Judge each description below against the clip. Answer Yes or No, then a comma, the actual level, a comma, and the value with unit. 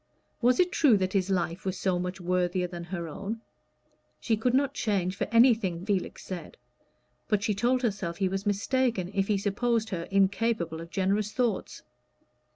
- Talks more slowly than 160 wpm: No, average, 170 wpm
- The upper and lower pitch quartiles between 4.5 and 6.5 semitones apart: No, average, 3.9 semitones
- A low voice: No, high, 195 Hz